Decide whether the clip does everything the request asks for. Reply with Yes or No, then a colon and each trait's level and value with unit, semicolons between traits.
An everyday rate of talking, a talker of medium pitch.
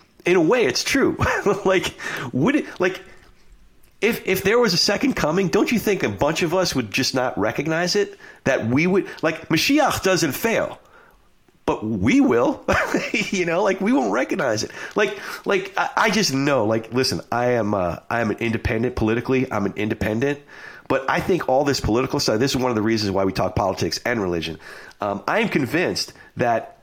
Yes: average, 195 wpm; medium, 145 Hz